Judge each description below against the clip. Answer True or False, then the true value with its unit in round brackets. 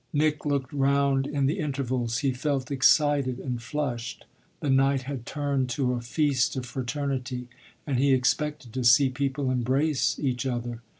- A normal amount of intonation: False (2.3 semitones)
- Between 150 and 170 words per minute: True (160 wpm)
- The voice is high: False (135 Hz)